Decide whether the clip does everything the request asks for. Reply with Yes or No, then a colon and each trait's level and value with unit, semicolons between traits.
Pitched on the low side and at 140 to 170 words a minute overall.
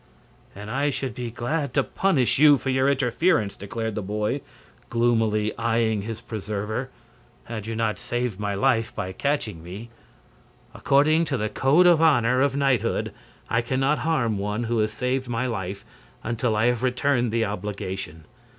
Yes: low, 115 Hz; average, 165 wpm